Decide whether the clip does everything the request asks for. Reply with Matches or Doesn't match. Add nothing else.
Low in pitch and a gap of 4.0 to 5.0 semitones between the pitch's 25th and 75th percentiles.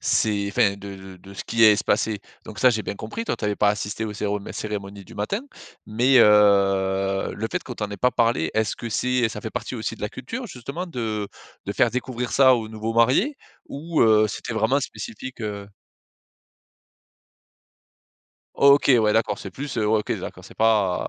Doesn't match